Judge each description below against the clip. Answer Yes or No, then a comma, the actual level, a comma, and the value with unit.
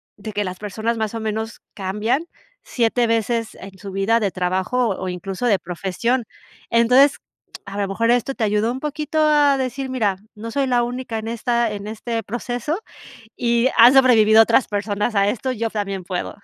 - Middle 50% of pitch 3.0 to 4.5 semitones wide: Yes, average, 3.3 semitones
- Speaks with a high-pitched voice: Yes, high, 225 Hz